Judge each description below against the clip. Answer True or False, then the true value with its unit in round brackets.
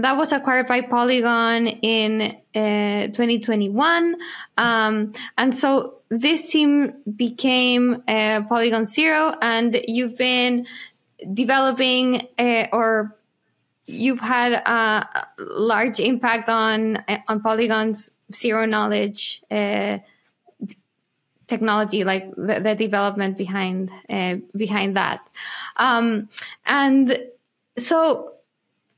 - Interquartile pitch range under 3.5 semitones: True (2.8 semitones)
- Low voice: False (230 Hz)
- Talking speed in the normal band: False (95 wpm)